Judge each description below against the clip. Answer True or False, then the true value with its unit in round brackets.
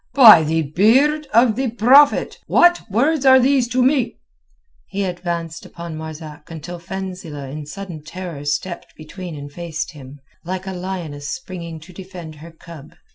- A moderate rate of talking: True (155 wpm)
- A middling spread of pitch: False (5.9 semitones)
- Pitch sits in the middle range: True (175 Hz)